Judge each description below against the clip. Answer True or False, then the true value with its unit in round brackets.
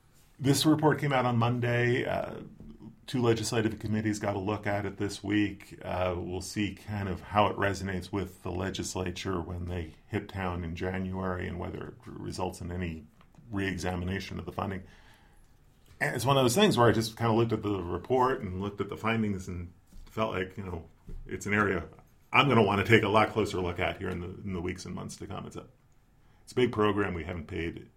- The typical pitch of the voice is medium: False (100 Hz)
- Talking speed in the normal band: False (220 wpm)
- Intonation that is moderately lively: True (3.4 semitones)